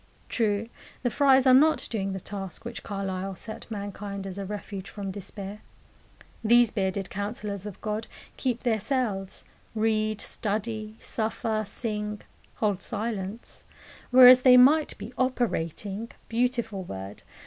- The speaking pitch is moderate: No, high, 215 Hz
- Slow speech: Yes, slow, 130 wpm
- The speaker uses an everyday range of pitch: Yes, average, 3.0 semitones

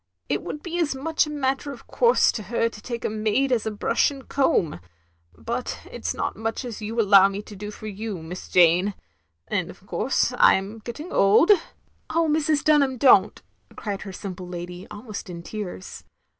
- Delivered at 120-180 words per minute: No, fast, 205 wpm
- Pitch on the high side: Yes, high, 215 Hz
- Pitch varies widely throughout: Yes, wide, 5.8 semitones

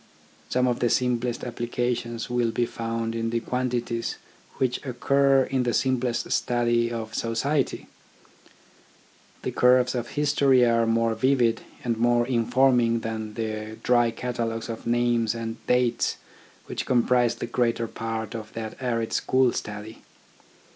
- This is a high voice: No, low, 120 Hz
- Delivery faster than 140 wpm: No, slow, 135 wpm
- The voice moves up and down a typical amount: No, narrow, 1.5 semitones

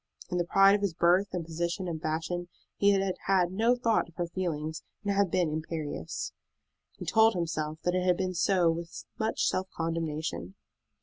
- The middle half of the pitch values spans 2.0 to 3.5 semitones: Yes, average, 2.8 semitones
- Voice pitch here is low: No, medium, 175 Hz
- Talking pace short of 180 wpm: No, average, 185 wpm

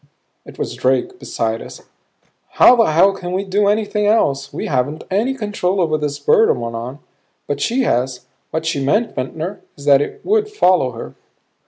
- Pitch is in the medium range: Yes, medium, 160 Hz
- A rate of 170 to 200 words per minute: Yes, average, 180 wpm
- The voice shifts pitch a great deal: Yes, wide, 7.2 semitones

